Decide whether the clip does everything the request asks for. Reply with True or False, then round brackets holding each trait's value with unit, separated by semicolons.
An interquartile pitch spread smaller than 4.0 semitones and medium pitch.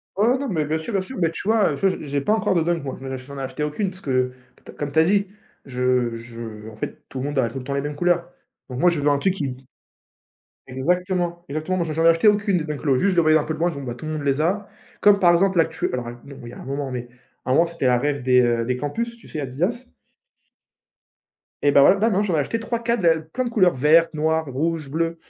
False (5.2 semitones; 155 Hz)